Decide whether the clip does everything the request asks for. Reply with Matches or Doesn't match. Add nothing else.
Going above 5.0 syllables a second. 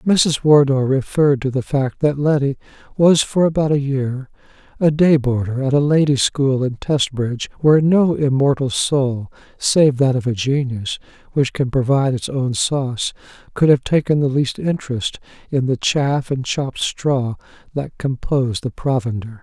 Doesn't match